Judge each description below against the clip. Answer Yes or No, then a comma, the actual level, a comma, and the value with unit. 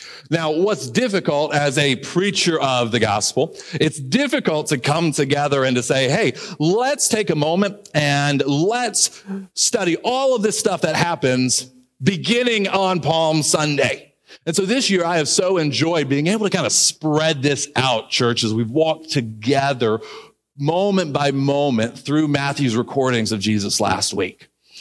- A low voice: No, medium, 150 Hz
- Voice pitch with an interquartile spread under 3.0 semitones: No, average, 5.3 semitones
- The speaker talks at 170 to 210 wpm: No, average, 160 wpm